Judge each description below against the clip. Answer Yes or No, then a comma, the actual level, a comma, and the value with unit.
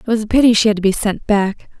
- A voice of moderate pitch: No, high, 215 Hz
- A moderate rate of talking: No, fast, 335 wpm